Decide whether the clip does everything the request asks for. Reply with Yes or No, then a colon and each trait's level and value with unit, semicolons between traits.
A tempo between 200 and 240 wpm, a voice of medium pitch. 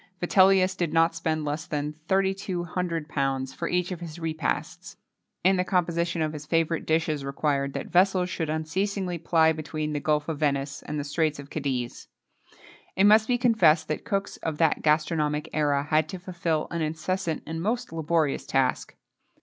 No: average, 180 wpm; medium, 160 Hz